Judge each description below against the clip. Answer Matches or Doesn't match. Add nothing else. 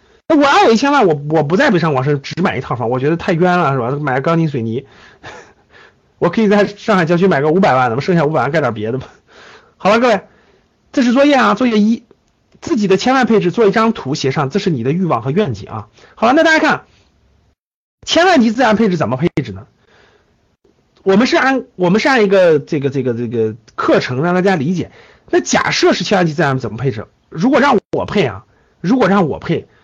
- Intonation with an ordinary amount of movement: Doesn't match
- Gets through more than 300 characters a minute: Matches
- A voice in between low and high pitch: Matches